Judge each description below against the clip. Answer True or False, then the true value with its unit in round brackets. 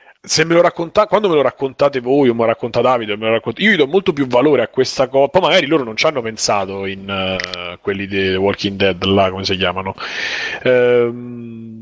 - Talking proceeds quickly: True (235 wpm)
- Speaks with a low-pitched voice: True (115 Hz)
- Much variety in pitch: True (5.9 semitones)